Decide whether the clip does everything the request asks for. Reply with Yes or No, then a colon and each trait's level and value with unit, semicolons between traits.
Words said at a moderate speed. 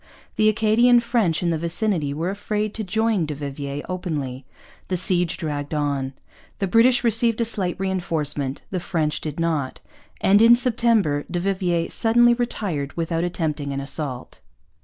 Yes: average, 155 wpm